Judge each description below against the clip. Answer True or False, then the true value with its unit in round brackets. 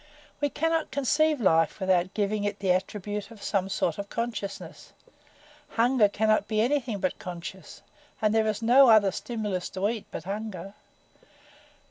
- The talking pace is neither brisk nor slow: True (150 wpm)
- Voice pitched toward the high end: True (210 Hz)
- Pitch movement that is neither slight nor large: True (3.1 semitones)